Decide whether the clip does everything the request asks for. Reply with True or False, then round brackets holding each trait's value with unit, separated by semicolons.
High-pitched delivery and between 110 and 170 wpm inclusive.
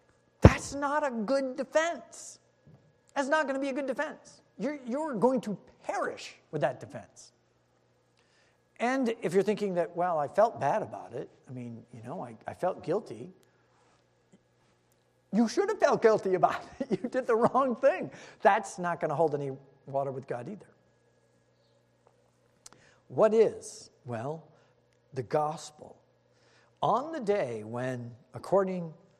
True (195 Hz; 155 wpm)